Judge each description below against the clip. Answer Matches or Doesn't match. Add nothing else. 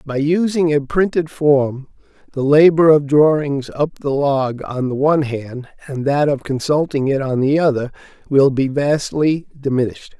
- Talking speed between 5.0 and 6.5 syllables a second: Doesn't match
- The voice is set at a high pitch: Doesn't match